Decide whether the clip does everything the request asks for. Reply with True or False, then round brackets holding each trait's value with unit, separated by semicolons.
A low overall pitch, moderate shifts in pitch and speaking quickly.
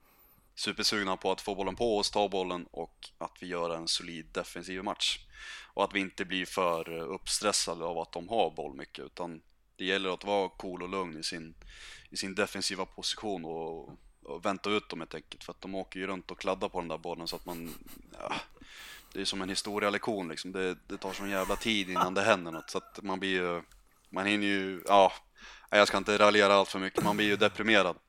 False (95 Hz; 2.3 semitones; 220 wpm)